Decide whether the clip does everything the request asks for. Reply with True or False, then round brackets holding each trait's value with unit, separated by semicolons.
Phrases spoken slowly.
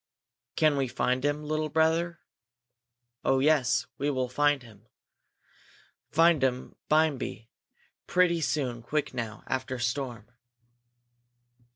True (100 wpm)